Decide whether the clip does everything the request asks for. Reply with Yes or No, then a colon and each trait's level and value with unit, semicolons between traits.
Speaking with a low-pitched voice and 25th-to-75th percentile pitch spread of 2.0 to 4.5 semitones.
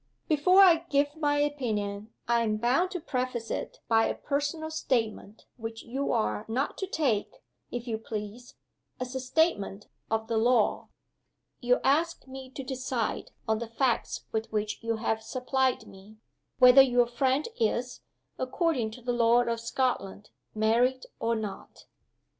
No: high, 245 Hz; average, 3.4 semitones